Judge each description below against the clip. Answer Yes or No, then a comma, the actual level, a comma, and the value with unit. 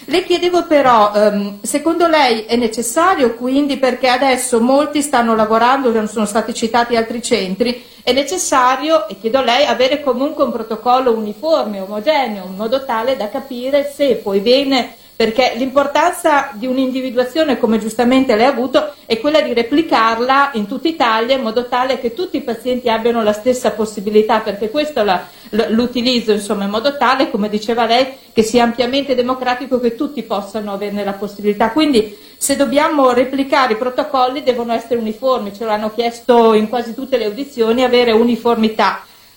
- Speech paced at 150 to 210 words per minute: Yes, average, 160 wpm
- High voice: Yes, high, 245 Hz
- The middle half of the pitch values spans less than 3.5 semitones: Yes, average, 3.1 semitones